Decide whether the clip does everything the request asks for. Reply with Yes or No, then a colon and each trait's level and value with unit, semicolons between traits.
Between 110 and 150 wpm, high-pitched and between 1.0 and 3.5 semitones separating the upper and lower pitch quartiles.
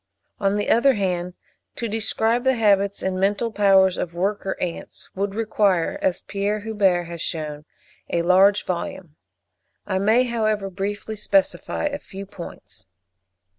Yes: average, 140 wpm; high, 200 Hz; average, 2.8 semitones